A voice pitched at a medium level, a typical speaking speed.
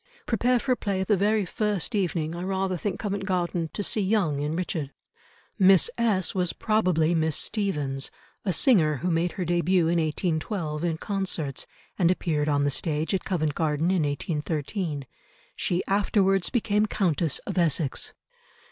Yes: medium, 175 Hz; average, 160 wpm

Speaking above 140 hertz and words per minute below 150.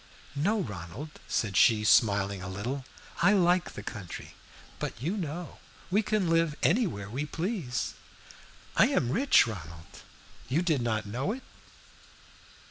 No: low, 135 Hz; slow, 135 wpm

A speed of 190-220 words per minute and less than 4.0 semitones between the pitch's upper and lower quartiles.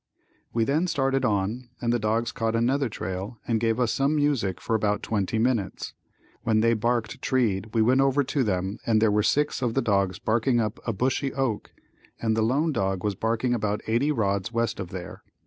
Yes: average, 200 wpm; average, 3.4 semitones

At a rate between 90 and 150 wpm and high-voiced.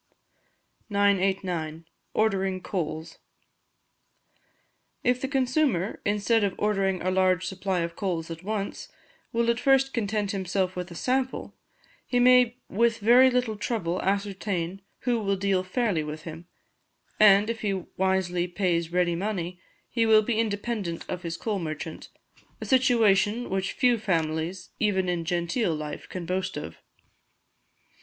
Yes: slow, 135 wpm; high, 195 Hz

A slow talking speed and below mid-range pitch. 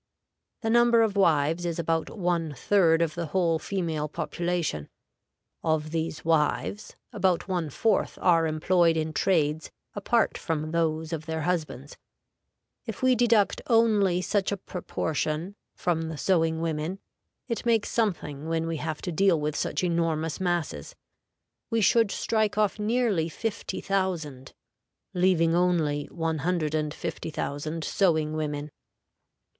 No: slow, 130 wpm; medium, 165 Hz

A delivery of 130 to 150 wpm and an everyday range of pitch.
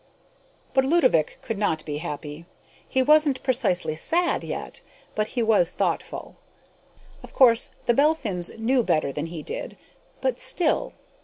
No: average, 140 wpm; wide, 8.3 semitones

